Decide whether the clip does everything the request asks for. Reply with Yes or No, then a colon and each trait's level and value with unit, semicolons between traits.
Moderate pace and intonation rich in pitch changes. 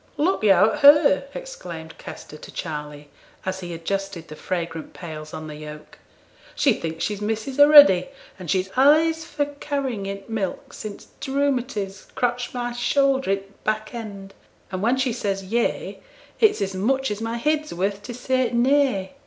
Yes: average, 175 wpm; wide, 6.2 semitones